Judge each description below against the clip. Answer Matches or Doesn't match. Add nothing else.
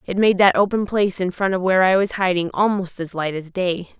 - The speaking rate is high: Matches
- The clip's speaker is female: Matches